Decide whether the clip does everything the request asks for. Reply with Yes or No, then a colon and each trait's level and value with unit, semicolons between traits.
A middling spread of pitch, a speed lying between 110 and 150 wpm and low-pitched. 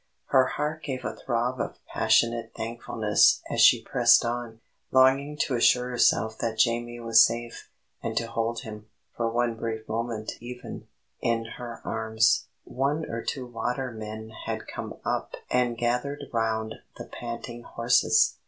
No: narrow, 1.7 semitones; average, 145 wpm; low, 120 Hz